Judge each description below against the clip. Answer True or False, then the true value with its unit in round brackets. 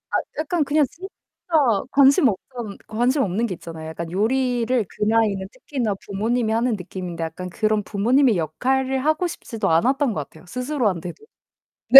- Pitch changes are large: True (5.7 semitones)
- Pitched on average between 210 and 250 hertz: True (225 Hz)